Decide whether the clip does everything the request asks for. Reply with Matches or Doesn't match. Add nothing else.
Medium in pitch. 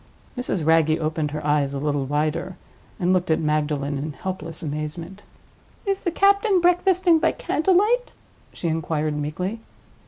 Matches